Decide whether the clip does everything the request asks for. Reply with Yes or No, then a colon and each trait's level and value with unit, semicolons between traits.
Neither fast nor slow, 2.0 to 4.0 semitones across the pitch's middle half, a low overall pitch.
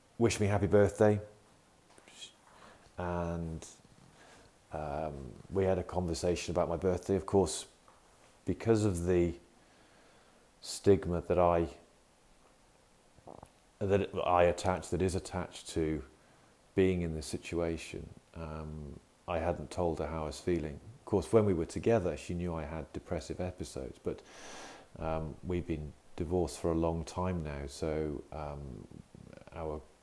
No: slow, 130 wpm; average, 2.7 semitones; very low, 85 Hz